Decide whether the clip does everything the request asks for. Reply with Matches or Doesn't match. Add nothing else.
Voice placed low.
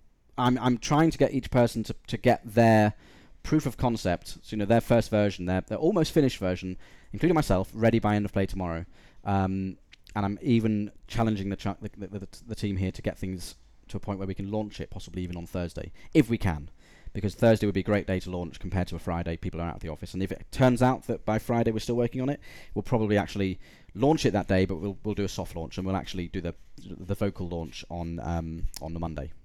Matches